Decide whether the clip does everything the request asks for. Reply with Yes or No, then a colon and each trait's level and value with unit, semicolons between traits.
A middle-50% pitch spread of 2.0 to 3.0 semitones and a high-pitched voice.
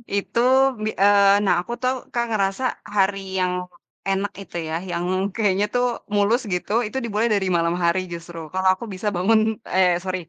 Yes: narrow, 2.5 semitones; high, 195 Hz